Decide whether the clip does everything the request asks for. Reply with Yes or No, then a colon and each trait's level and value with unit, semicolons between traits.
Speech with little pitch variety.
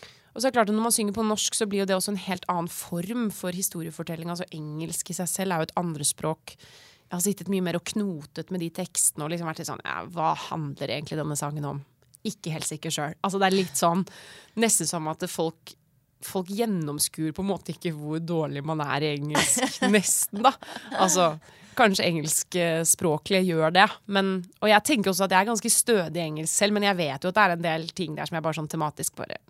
No: average, 3.7 semitones